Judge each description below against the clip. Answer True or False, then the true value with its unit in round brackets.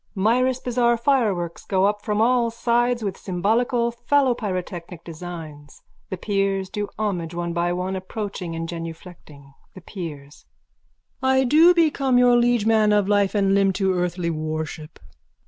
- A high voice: True (195 Hz)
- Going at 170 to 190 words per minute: False (145 wpm)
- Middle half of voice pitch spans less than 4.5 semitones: False (5.4 semitones)